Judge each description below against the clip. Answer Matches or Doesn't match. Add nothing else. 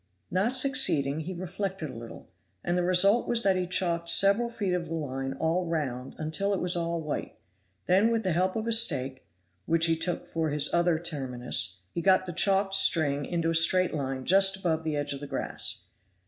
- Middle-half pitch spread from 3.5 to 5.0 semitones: Matches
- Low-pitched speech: Doesn't match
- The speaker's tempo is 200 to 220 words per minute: Matches